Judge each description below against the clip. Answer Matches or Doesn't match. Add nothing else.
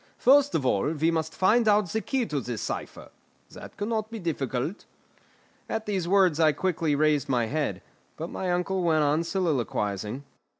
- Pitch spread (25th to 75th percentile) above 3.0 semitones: Matches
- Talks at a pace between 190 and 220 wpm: Doesn't match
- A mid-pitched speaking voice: Matches